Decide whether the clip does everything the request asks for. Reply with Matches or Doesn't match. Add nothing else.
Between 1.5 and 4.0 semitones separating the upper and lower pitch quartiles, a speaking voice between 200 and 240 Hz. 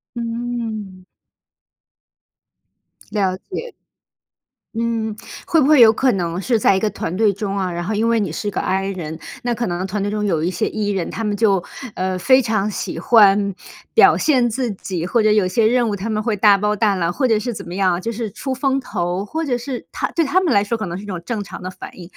Matches